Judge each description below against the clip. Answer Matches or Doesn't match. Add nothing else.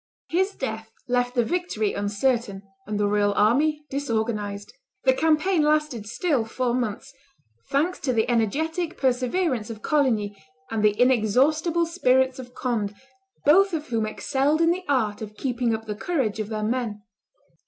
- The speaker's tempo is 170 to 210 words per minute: Doesn't match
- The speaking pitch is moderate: Doesn't match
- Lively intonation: Matches